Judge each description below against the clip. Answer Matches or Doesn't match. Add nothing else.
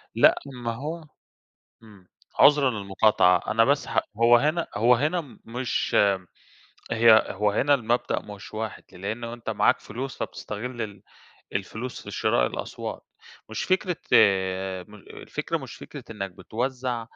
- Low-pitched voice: Matches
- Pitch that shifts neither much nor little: Matches